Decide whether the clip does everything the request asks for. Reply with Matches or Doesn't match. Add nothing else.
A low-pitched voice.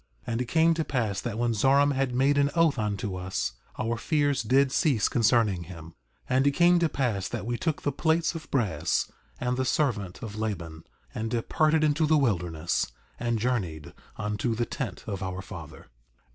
Matches